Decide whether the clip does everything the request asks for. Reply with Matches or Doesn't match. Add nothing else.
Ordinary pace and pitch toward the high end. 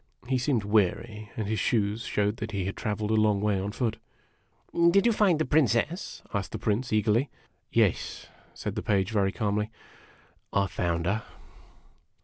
Doesn't match